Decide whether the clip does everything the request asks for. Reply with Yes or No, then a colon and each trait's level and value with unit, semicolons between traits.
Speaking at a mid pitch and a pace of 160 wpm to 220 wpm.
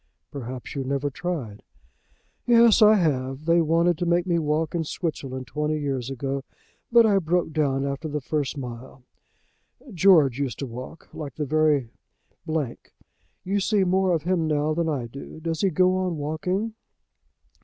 Yes: medium, 155 Hz; average, 165 wpm